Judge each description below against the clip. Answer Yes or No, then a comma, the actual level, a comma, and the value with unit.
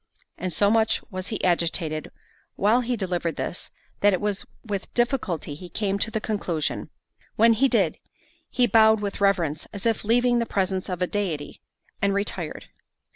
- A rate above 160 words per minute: Yes, average, 170 wpm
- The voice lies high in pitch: Yes, high, 200 Hz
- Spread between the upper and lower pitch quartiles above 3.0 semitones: Yes, average, 3.6 semitones